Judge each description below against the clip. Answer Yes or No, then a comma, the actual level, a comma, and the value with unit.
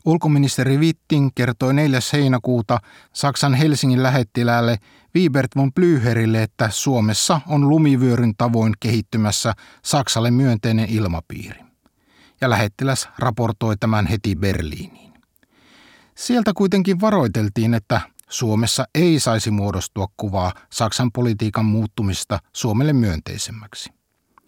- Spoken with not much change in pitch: No, average, 3.9 semitones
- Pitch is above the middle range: No, low, 120 Hz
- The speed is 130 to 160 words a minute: No, average, 100 wpm